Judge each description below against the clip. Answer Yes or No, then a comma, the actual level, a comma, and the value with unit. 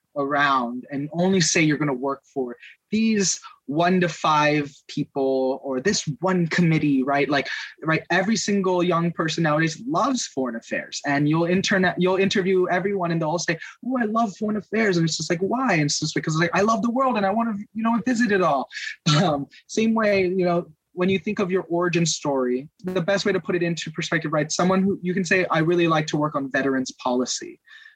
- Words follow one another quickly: Yes, fast, 220 wpm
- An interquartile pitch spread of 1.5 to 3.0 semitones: No, average, 4.7 semitones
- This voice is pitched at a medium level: Yes, medium, 175 Hz